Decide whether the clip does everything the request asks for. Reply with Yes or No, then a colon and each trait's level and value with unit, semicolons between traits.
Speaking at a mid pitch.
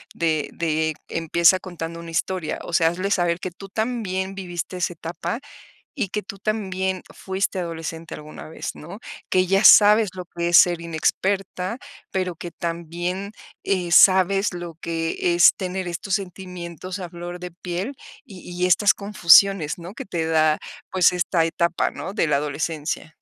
Yes: medium, 175 Hz